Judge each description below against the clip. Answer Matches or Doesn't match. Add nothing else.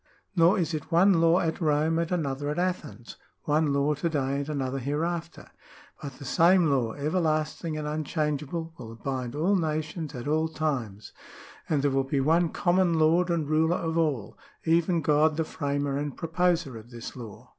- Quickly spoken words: Doesn't match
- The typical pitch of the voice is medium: Matches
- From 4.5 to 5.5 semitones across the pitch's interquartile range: Doesn't match